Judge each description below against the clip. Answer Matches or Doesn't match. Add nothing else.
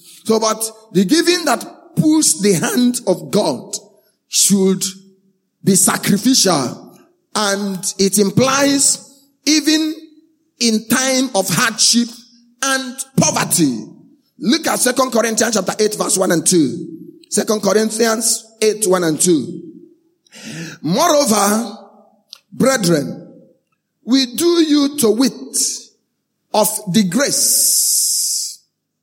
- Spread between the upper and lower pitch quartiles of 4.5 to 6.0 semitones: Matches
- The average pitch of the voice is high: Matches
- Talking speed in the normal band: Doesn't match